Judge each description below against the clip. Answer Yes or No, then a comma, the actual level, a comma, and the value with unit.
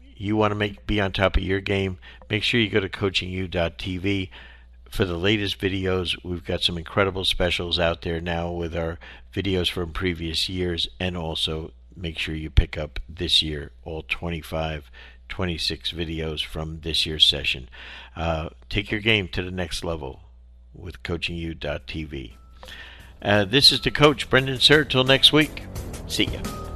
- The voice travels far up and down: No, average, 3.6 semitones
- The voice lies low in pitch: Yes, very low, 85 Hz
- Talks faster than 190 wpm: No, average, 165 wpm